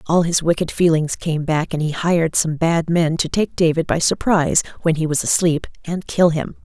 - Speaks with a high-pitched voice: No, medium, 165 Hz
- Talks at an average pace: No, fast, 215 wpm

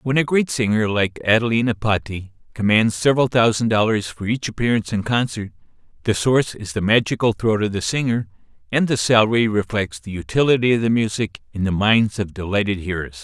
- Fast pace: No, average, 180 wpm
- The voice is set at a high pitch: No, low, 110 Hz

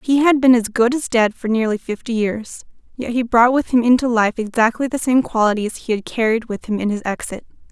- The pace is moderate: No, fast, 235 wpm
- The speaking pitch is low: No, high, 235 Hz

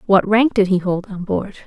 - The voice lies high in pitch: Yes, high, 200 Hz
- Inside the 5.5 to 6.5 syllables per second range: No, 5.0 syllables/s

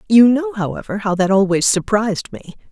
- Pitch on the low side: No, high, 205 Hz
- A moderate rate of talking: Yes, average, 175 wpm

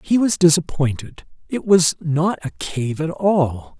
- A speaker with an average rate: Yes, average, 160 wpm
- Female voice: No, male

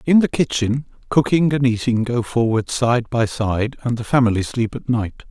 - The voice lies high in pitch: No, low, 120 Hz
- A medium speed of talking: Yes, average, 190 wpm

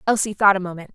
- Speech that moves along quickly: Yes, fast, 255 wpm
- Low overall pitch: No, high, 195 Hz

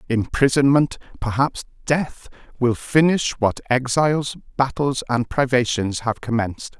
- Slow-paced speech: Yes, slow, 105 wpm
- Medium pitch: No, low, 130 Hz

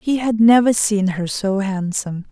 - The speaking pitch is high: Yes, high, 205 Hz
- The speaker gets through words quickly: No, average, 180 wpm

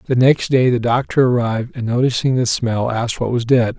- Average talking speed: No, fast, 220 wpm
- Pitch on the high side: No, low, 120 Hz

